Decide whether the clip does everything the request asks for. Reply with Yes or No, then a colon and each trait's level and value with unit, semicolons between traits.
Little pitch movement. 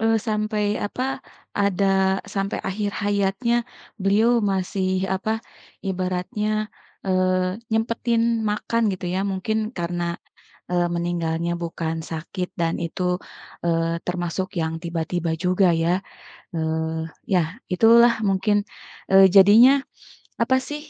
No: average, 3.5 semitones